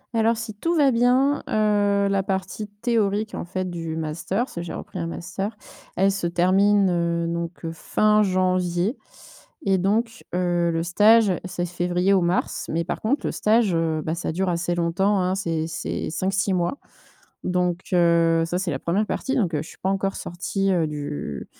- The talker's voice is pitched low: No, medium, 185 Hz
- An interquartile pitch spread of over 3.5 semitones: No, average, 3.2 semitones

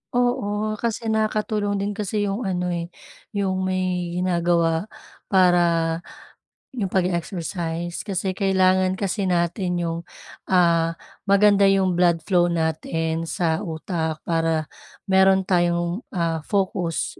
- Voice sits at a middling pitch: Yes, medium, 180 Hz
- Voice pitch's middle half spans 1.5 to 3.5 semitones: Yes, narrow, 2.5 semitones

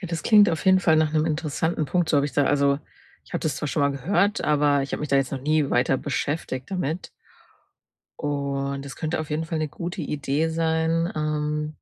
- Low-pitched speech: No, medium, 150 Hz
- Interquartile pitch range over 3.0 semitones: No, narrow, 2.4 semitones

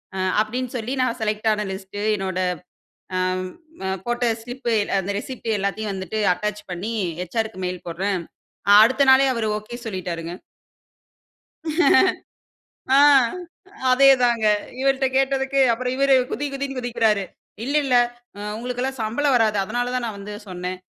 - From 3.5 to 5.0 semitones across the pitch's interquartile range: Yes, average, 4.5 semitones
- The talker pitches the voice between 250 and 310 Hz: No, high, 225 Hz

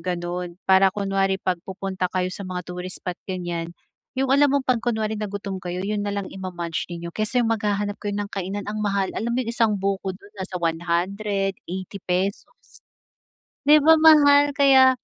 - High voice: Yes, high, 195 Hz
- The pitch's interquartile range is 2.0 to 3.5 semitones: Yes, average, 2.7 semitones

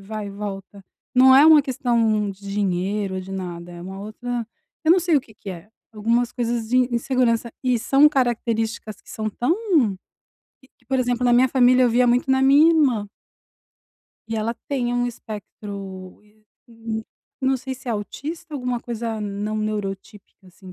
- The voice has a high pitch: Yes, high, 230 Hz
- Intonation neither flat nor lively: Yes, average, 3.5 semitones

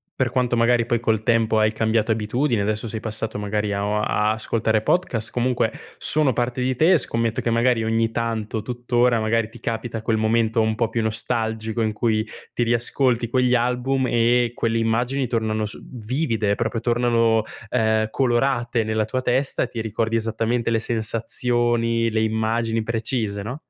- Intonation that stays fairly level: Yes, narrow, 1.7 semitones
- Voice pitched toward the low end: Yes, low, 115 Hz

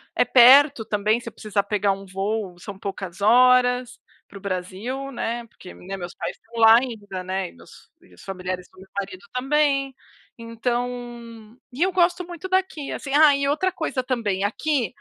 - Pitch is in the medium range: No, high, 230 Hz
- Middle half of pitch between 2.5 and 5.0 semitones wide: No, wide, 5.5 semitones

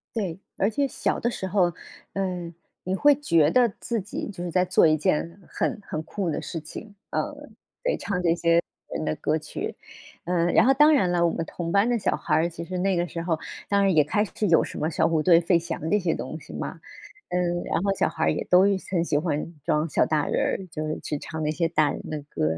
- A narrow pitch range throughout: No, average, 3.4 semitones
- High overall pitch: No, medium, 175 Hz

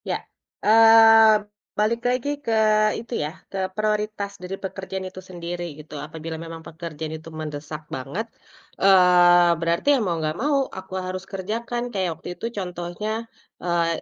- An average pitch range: Yes, average, 4.1 semitones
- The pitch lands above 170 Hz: Yes, medium, 185 Hz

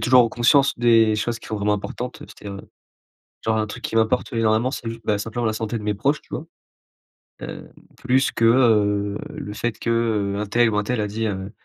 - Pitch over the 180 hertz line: No, low, 110 Hz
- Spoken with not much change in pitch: Yes, narrow, 2.3 semitones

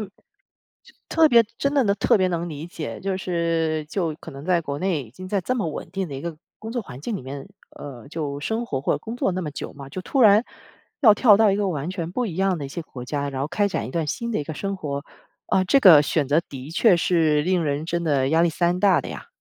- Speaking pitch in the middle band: Yes, medium, 170 Hz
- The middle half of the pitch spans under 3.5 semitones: No, average, 5.1 semitones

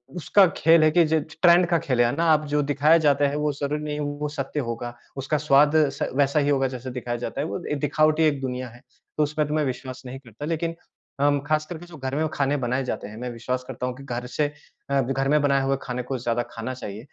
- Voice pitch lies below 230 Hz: Yes, medium, 140 Hz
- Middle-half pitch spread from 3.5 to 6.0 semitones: No, average, 3.1 semitones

